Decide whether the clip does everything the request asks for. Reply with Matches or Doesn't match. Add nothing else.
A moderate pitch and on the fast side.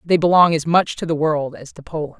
Matches